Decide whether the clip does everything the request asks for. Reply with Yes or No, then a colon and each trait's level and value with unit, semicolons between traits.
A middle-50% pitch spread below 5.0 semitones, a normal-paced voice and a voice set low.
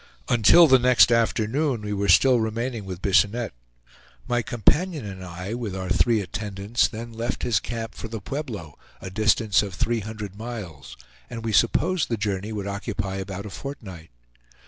Yes: average, 3.4 semitones; average, 170 wpm; low, 110 Hz